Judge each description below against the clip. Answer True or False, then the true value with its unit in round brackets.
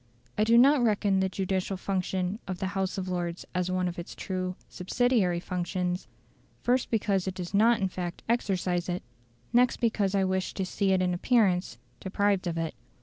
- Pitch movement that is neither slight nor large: False (2.2 semitones)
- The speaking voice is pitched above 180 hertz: True (190 Hz)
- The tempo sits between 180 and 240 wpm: True (185 wpm)